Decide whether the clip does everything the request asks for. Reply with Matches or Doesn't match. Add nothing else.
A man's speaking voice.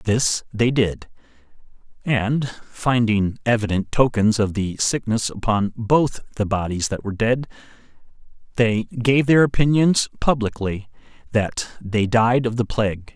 Matches